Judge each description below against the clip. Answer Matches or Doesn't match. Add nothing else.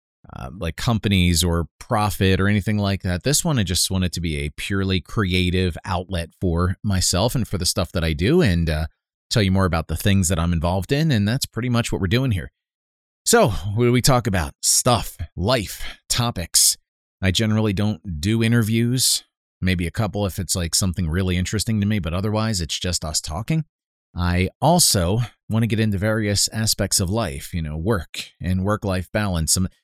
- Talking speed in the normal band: Matches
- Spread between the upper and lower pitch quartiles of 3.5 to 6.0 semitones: Matches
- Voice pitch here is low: Matches